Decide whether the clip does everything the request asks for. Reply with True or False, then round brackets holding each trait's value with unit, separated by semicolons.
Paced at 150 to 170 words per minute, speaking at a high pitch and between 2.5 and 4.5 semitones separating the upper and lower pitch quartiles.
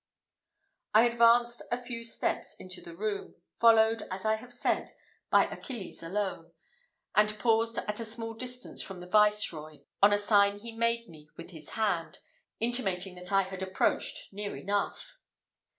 True (155 wpm; 210 Hz; 3.4 semitones)